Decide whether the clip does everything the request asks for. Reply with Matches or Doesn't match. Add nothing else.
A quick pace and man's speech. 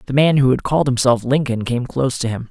Matches